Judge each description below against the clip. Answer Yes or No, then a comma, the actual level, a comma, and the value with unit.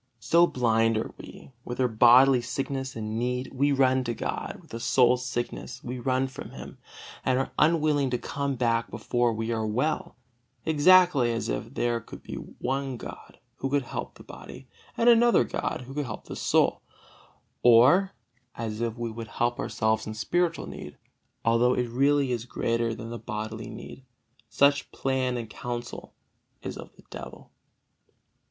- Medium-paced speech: Yes, average, 170 wpm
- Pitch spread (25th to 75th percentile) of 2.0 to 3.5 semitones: Yes, average, 2.8 semitones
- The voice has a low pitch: Yes, low, 125 Hz